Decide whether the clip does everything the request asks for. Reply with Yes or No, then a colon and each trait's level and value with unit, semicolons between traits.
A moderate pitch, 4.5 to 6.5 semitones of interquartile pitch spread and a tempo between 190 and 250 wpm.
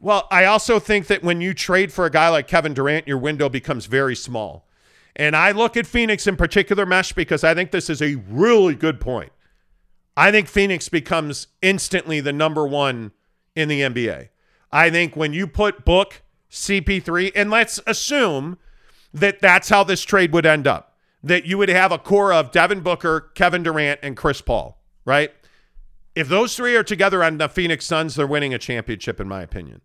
Yes: medium, 165 Hz; average, 5.3 semitones; average, 195 wpm